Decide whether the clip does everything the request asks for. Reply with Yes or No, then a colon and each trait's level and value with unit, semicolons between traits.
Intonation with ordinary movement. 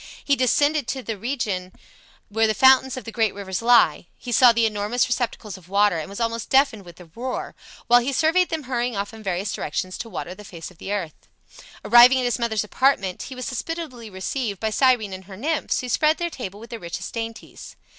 Yes: average, 4.4 semitones